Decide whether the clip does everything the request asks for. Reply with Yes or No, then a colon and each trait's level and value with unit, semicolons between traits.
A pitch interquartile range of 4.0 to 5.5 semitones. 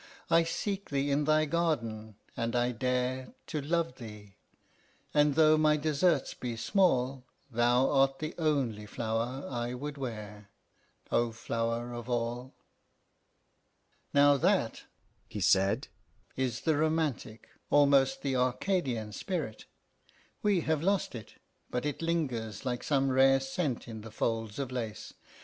Yes: average, 4.5 semitones